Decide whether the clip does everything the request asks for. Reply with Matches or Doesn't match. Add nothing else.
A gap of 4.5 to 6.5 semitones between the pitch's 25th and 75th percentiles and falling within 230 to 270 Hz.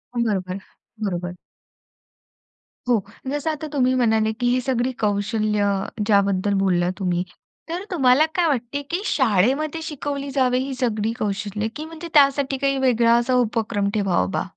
Matches